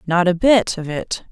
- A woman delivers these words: Yes, female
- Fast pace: Yes, fast, 230 wpm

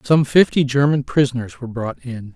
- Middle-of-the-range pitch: No, low, 130 Hz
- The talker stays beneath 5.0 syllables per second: No, 5.5 syllables/s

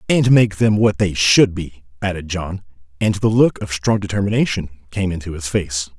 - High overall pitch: No, very low, 95 Hz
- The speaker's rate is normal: Yes, average, 190 wpm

